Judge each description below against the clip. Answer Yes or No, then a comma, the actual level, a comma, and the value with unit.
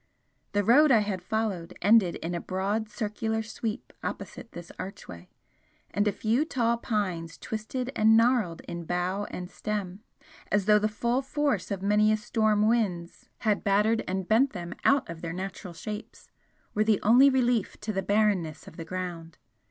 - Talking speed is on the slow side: No, average, 165 wpm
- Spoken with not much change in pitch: No, average, 3.4 semitones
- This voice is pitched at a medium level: No, high, 210 Hz